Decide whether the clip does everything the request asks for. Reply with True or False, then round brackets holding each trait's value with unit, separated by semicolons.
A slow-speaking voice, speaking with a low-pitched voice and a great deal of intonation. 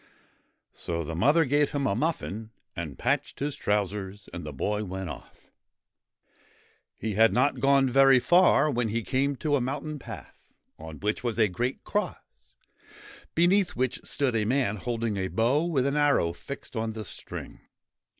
False (165 wpm; 120 Hz; 5.7 semitones)